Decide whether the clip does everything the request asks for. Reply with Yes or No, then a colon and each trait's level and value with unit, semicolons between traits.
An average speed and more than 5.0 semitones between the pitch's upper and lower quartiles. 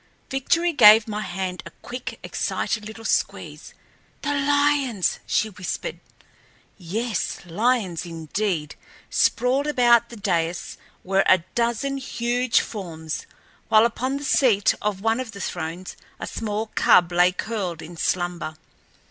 No: slow, 130 wpm; wide, 5.5 semitones